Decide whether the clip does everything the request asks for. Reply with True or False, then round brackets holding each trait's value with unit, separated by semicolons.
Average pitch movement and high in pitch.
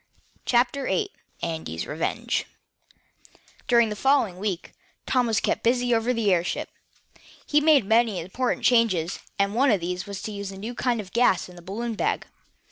True (4.6 semitones; 220 Hz)